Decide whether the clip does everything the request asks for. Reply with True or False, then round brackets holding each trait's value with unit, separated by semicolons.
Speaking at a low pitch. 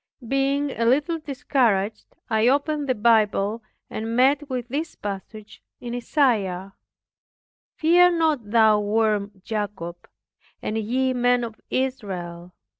False (230 Hz)